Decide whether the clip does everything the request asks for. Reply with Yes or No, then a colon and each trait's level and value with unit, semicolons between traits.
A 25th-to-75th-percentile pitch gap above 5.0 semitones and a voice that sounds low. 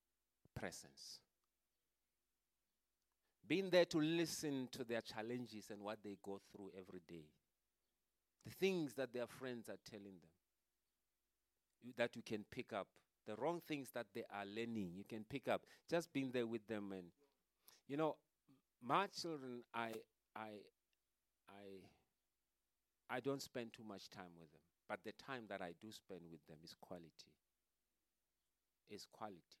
Yes: wide, 5.5 semitones; low, 110 Hz